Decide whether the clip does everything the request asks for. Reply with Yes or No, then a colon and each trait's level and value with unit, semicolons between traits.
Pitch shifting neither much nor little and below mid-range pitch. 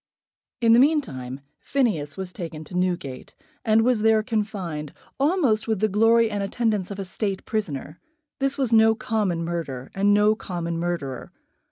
No: average, 4.7 semitones; high, 205 Hz